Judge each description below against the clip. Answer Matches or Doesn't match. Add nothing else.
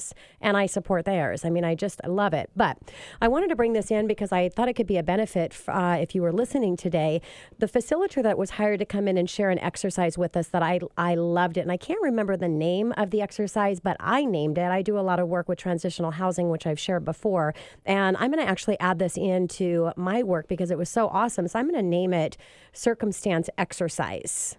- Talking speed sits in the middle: Doesn't match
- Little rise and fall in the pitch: Doesn't match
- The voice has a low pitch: Doesn't match